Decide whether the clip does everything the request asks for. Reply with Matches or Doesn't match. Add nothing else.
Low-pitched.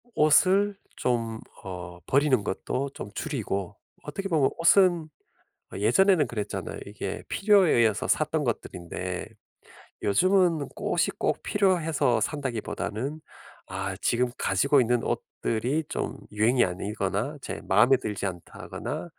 Matches